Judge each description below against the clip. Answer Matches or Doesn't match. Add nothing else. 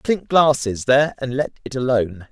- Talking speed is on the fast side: Doesn't match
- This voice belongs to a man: Matches